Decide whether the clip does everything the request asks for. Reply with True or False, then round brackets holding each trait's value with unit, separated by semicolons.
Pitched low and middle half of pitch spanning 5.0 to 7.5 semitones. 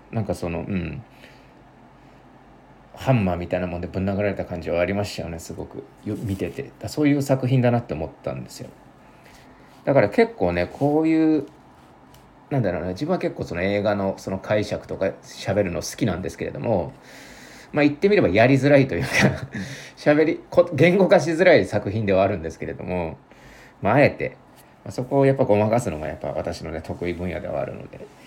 False (100 Hz; 8.2 semitones)